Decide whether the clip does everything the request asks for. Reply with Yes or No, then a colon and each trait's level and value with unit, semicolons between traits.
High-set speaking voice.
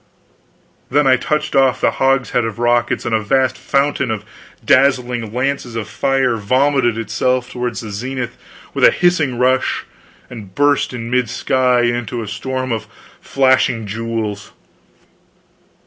No: low, 125 Hz